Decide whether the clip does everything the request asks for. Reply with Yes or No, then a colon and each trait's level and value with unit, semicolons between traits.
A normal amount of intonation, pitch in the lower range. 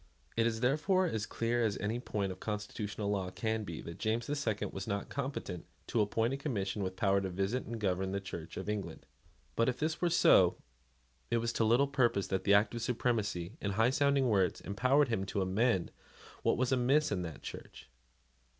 Yes: average, 4.1 semitones; low, 110 Hz